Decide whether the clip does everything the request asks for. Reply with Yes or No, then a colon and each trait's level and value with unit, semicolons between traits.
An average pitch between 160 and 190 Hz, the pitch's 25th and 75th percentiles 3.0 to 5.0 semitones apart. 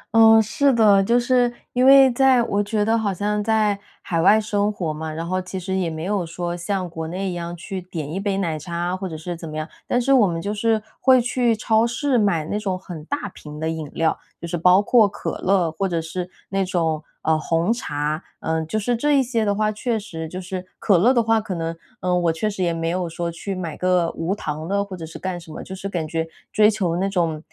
Yes: medium, 185 Hz; average, 4.3 semitones